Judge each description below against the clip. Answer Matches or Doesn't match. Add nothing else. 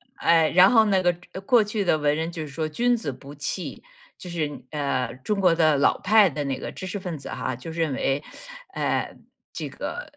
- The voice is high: Doesn't match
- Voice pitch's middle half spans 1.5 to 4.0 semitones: Doesn't match